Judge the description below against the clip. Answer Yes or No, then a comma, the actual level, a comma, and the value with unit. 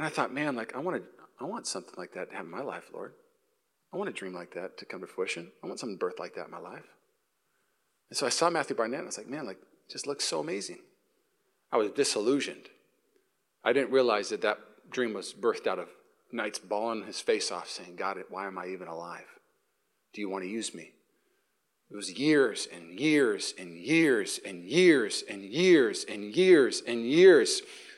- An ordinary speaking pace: No, fast, 215 wpm